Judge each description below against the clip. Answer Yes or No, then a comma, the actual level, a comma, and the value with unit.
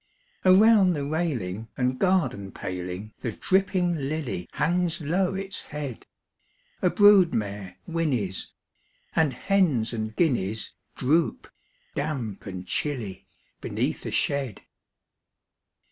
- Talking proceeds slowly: Yes, slow, 105 wpm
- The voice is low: No, medium, 145 Hz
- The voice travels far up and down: Yes, wide, 8.3 semitones